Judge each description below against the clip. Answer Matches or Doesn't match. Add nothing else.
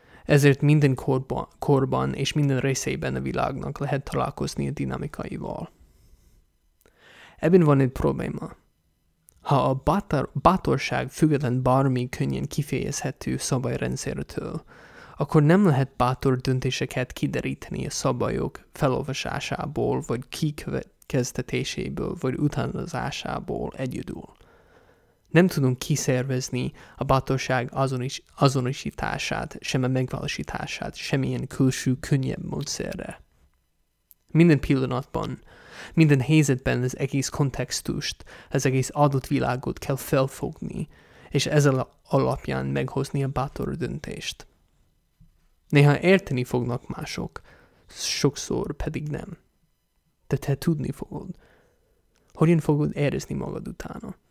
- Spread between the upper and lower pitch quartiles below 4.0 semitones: Matches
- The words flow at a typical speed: Doesn't match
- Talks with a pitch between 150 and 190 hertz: Doesn't match